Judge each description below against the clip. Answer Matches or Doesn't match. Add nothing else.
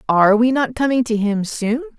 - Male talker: Doesn't match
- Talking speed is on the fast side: Matches